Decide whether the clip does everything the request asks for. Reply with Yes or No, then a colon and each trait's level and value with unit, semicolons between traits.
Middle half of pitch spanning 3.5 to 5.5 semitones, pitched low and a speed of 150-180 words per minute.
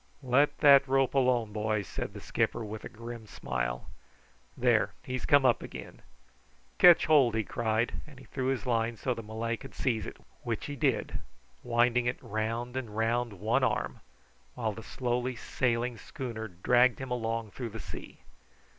No: narrow, 2.6 semitones; low, 120 Hz; average, 170 wpm